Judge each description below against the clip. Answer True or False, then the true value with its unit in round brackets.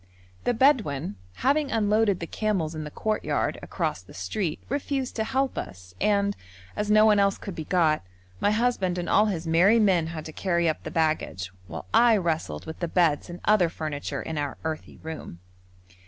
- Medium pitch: True (180 Hz)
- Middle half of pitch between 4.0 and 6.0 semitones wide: True (5.2 semitones)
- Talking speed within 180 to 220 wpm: True (185 wpm)